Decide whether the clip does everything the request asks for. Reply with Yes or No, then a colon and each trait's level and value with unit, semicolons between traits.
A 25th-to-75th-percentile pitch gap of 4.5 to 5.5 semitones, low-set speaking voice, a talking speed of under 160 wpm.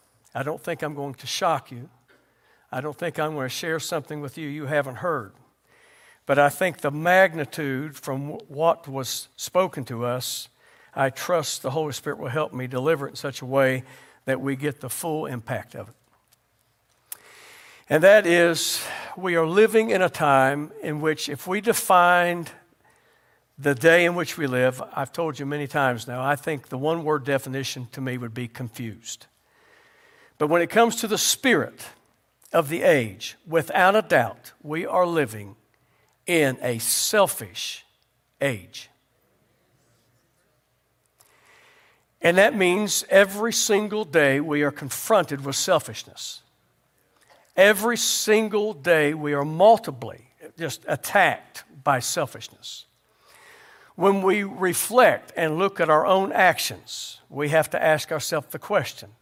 No: average, 4.9 semitones; medium, 150 Hz; average, 150 wpm